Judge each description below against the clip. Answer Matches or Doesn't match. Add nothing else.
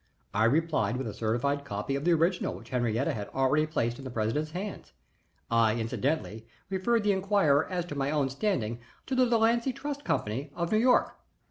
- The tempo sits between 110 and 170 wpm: Doesn't match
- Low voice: Doesn't match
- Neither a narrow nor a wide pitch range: Doesn't match